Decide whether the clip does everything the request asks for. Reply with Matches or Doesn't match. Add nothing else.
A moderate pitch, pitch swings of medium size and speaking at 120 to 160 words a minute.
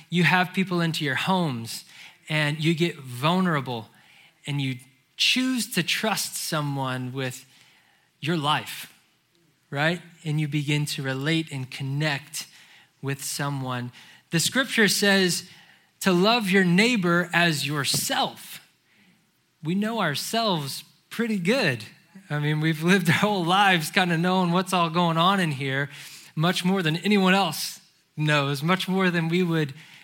Matches